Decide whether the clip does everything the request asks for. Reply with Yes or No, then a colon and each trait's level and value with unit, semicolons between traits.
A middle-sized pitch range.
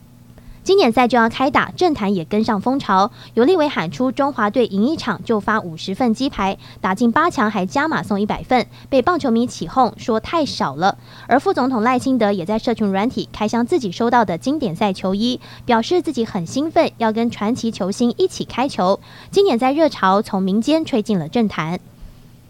Yes: average, 4.4 semitones